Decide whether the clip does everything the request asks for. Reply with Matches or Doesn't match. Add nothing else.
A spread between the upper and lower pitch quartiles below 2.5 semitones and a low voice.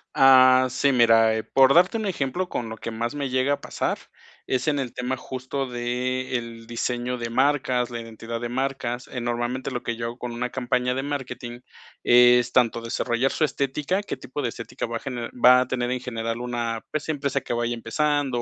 Matches